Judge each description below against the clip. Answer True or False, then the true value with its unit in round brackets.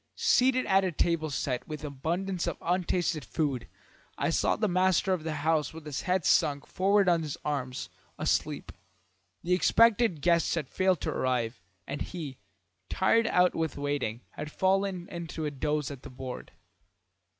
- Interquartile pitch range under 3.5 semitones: False (4.3 semitones)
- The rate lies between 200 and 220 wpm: False (160 wpm)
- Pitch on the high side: False (165 Hz)